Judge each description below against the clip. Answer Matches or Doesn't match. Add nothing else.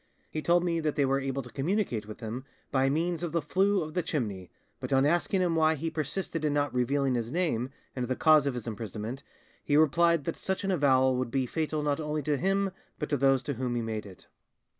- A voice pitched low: Doesn't match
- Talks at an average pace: Doesn't match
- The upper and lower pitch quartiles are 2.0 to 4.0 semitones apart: Doesn't match